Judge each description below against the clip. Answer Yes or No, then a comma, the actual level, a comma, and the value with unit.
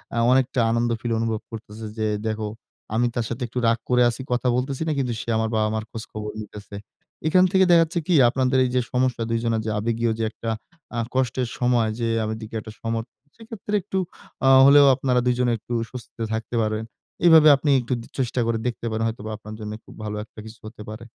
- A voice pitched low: Yes, low, 115 Hz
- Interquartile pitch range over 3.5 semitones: No, average, 2.7 semitones